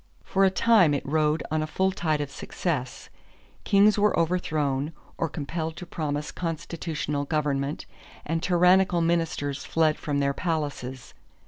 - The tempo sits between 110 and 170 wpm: Yes, average, 140 wpm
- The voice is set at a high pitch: No, medium, 155 Hz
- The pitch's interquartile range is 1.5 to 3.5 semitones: Yes, average, 3.2 semitones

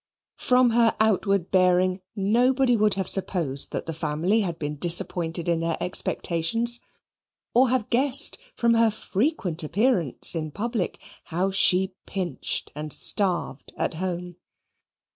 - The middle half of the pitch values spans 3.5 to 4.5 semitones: No, average, 5.3 semitones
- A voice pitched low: No, high, 190 Hz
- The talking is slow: Yes, slow, 130 wpm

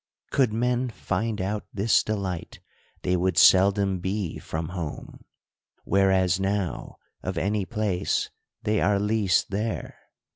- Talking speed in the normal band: No, slow, 120 wpm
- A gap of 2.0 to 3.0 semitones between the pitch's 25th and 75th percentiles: Yes, narrow, 2.5 semitones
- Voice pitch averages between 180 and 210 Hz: No, low, 100 Hz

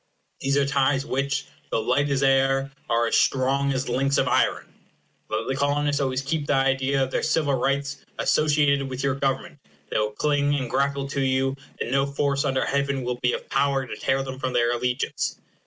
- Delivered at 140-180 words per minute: No, average, 200 wpm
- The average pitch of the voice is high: No, low, 135 Hz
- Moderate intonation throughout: No, narrow, 1.0 semitones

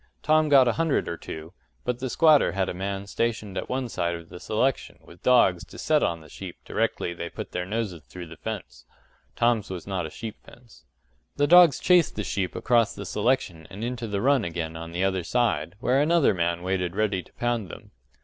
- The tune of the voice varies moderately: No, wide, 6.0 semitones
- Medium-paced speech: No, fast, 215 wpm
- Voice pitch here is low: Yes, low, 105 Hz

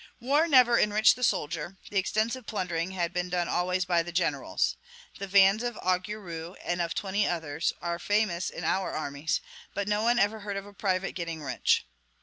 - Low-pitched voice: No, high, 190 Hz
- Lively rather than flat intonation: No, average, 3.5 semitones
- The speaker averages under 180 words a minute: No, average, 185 wpm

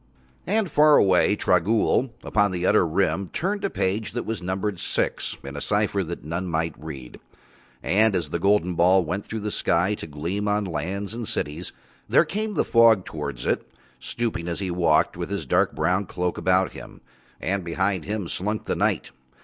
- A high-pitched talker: No, very low, 95 Hz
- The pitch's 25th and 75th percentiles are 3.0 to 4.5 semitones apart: Yes, average, 3.5 semitones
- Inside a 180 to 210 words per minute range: Yes, average, 185 wpm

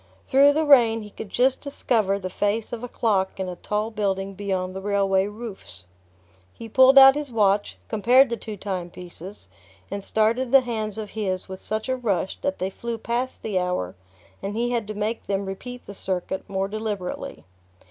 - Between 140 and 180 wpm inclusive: No, average, 190 wpm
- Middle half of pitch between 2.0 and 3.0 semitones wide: No, average, 3.6 semitones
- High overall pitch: Yes, high, 210 Hz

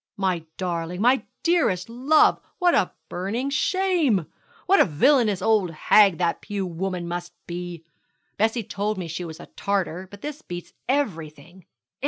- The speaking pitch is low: No, high, 190 Hz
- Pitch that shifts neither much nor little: No, wide, 5.8 semitones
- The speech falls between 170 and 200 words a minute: No, average, 150 wpm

